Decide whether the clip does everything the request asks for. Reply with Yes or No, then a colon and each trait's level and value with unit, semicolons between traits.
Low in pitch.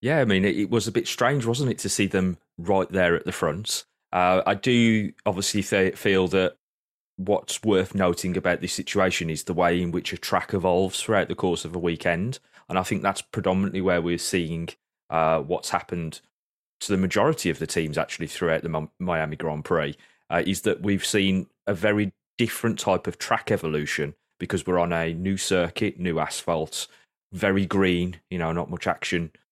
Yes: very low, 95 Hz